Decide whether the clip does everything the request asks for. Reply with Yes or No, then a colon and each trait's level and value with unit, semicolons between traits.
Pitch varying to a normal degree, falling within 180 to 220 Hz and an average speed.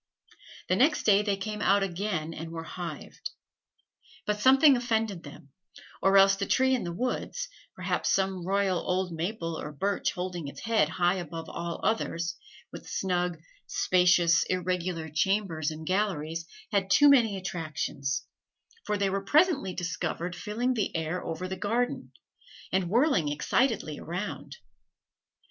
Yes: average, 4.0 semitones; medium, 185 Hz; average, 145 wpm